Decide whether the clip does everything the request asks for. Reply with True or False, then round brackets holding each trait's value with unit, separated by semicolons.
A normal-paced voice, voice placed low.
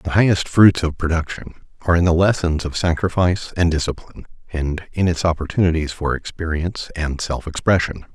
True (160 wpm; 85 Hz)